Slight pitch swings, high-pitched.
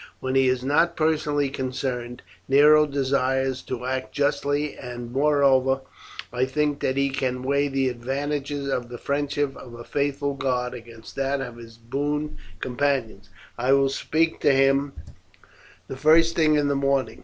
No: narrow, 2.0 semitones; low, 135 Hz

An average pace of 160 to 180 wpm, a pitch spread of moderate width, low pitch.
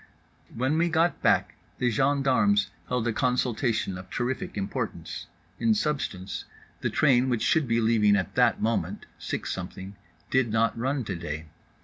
No: average, 150 wpm; average, 4.2 semitones; low, 120 Hz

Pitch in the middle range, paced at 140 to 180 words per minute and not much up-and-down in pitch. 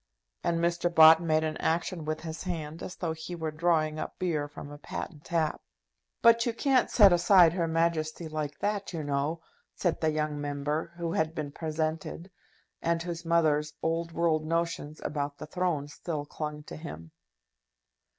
Yes: medium, 160 Hz; average, 170 wpm; narrow, 1.9 semitones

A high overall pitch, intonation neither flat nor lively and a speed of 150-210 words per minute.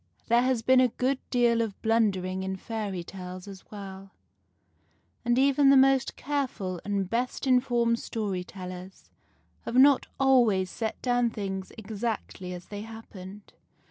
No: high, 220 Hz; average, 4.5 semitones; average, 140 wpm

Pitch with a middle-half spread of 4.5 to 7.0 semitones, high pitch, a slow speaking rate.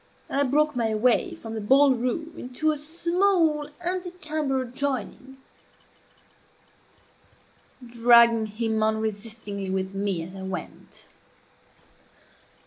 Yes: wide, 5.6 semitones; high, 245 Hz; slow, 110 wpm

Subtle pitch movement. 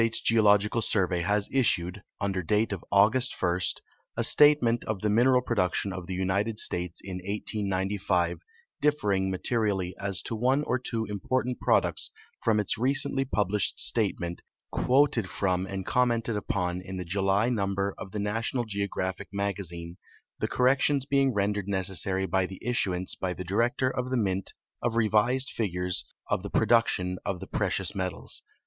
No: average, 3.8 semitones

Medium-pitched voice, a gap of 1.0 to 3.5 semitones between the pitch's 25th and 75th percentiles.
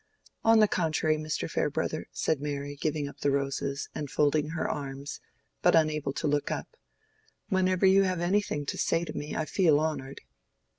Yes: medium, 155 Hz; average, 2.8 semitones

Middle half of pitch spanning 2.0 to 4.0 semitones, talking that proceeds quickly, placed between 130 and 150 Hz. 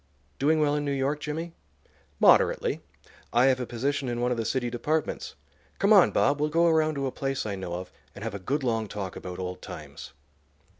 No: average, 4.8 semitones; fast, 210 wpm; low, 135 Hz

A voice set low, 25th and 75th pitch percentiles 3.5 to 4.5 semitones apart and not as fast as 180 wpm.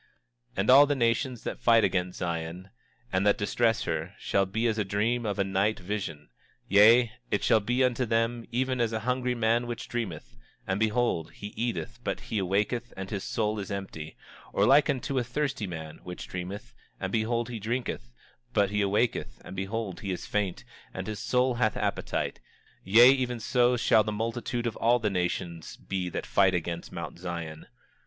No: low, 110 Hz; average, 4.0 semitones; average, 190 wpm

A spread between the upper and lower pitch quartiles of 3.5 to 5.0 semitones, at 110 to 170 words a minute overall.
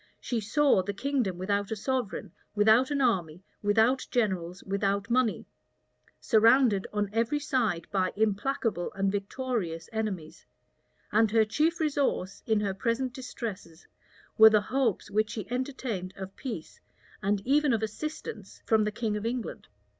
Yes: average, 4.3 semitones; average, 145 wpm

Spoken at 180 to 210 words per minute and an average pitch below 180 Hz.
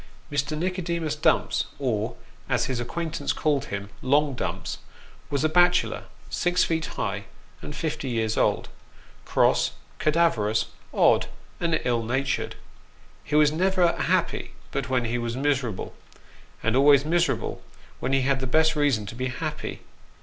No: average, 145 wpm; medium, 140 Hz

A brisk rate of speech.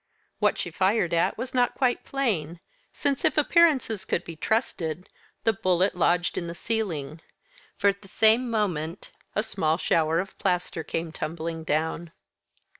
No: average, 155 wpm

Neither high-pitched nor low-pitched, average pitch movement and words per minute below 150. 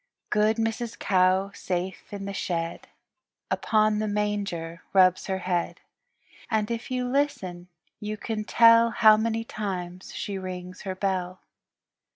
No: high, 200 Hz; average, 3.1 semitones; slow, 135 wpm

